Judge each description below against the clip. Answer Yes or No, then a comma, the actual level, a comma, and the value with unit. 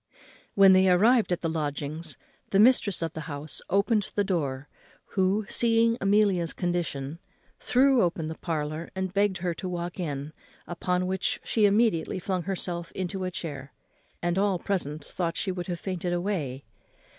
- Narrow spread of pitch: No, average, 3.4 semitones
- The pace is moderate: Yes, average, 160 wpm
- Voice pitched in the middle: Yes, medium, 180 Hz